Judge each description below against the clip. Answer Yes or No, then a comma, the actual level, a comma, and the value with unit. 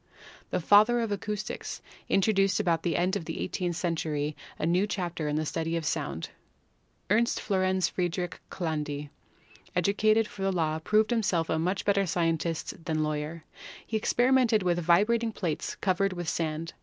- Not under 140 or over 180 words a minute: Yes, average, 160 wpm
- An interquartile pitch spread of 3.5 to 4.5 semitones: Yes, average, 3.9 semitones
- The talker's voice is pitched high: No, medium, 180 Hz